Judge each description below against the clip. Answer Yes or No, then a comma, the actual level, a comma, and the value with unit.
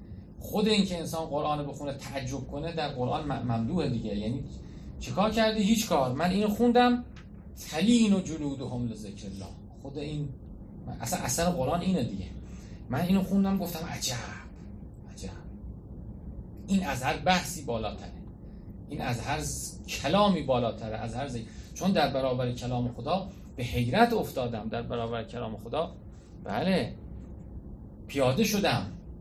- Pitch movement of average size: No, wide, 7.5 semitones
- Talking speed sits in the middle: Yes, average, 135 wpm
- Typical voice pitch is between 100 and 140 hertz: Yes, low, 135 Hz